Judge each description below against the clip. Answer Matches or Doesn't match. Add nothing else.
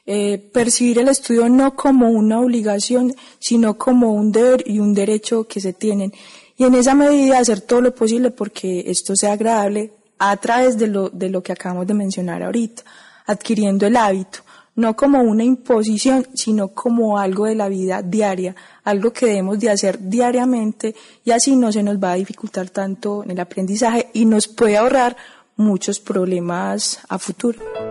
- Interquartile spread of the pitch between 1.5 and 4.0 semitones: Matches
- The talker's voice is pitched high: Matches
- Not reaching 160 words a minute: Doesn't match